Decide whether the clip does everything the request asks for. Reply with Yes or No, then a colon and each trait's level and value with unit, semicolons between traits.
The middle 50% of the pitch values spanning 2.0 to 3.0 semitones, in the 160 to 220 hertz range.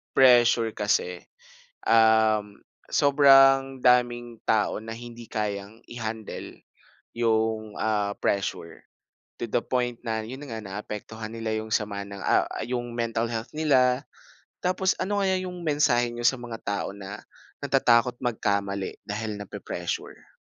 No: average, 2.7 semitones; low, 115 Hz